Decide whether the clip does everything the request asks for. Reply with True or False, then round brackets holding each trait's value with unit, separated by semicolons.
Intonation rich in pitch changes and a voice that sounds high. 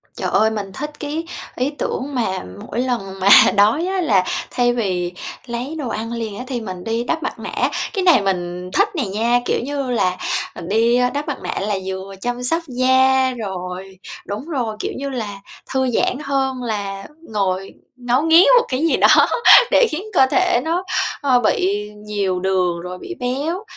True (5.9 semitones; 240 Hz)